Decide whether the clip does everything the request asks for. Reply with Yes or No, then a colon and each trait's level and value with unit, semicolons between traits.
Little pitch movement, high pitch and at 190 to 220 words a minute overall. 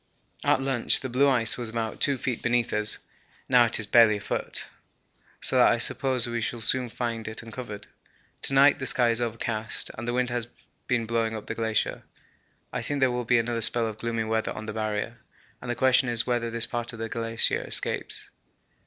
No: narrow, 1.6 semitones; low, 115 Hz; fast, 205 wpm